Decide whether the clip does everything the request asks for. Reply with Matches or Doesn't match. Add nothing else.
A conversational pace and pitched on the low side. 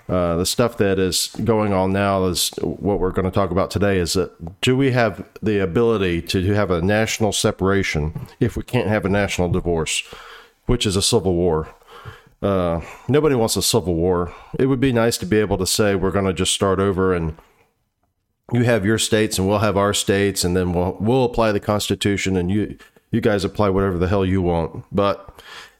Doesn't match